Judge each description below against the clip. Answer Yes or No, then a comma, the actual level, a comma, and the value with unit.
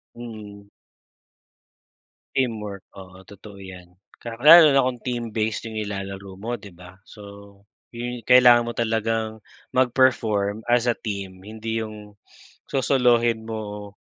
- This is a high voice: No, low, 110 Hz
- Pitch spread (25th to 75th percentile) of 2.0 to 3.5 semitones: Yes, average, 2.9 semitones